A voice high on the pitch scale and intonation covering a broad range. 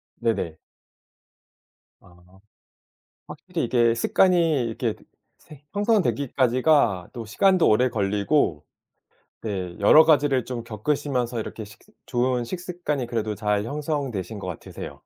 No: low, 120 Hz; wide, 6.0 semitones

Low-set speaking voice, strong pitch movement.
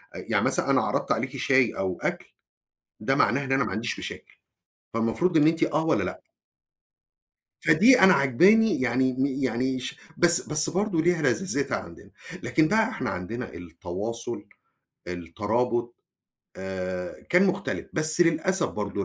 Yes: low, 130 Hz; wide, 6.4 semitones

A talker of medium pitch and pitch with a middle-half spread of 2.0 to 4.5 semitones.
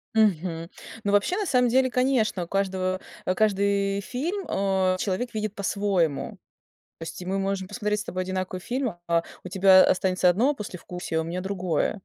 No: high, 195 Hz; average, 2.7 semitones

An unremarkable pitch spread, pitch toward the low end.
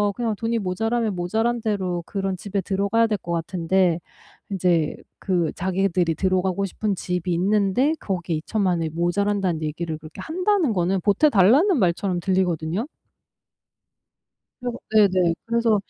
No: average, 3.7 semitones; high, 190 Hz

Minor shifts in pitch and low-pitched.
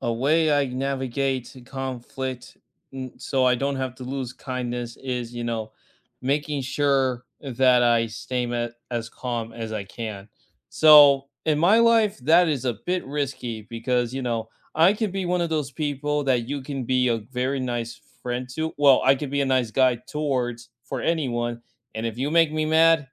No: average, 3.2 semitones; low, 130 Hz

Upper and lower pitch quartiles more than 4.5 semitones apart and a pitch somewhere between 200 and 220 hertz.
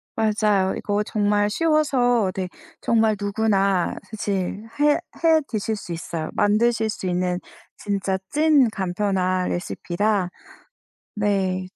No: average, 2.8 semitones; high, 205 Hz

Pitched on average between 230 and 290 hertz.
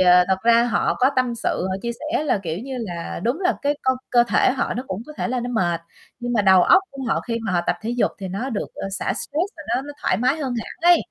Yes: high, 240 Hz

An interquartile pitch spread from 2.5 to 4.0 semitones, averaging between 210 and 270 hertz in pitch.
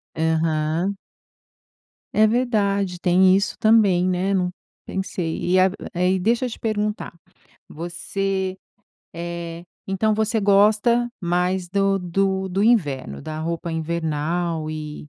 No: average, 3.1 semitones; medium, 185 Hz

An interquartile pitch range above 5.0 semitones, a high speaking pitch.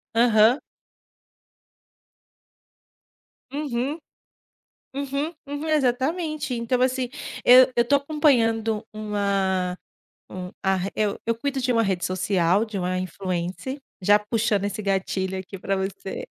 Yes: wide, 5.4 semitones; high, 220 Hz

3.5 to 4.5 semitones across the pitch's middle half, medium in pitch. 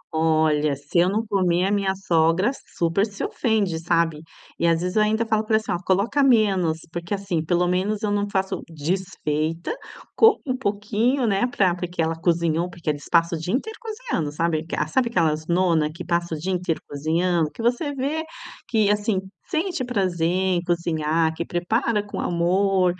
Yes: average, 4.2 semitones; medium, 180 Hz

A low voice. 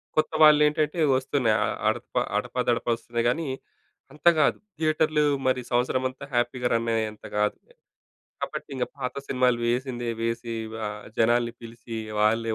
Yes: low, 125 Hz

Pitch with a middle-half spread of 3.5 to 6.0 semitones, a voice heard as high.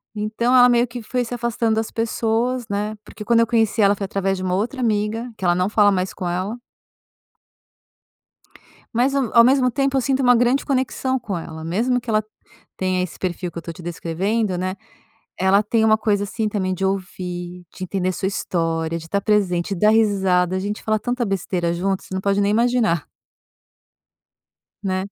Yes: average, 3.9 semitones; high, 205 Hz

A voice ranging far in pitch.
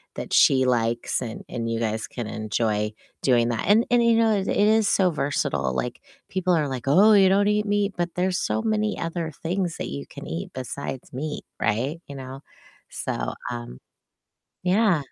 Yes: wide, 8.9 semitones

